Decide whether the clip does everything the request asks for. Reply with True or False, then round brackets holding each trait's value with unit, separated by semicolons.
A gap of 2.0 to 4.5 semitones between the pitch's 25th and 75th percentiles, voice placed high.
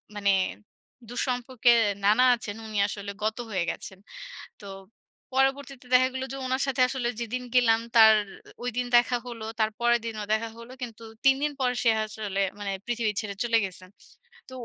True (2.8 semitones; 235 Hz)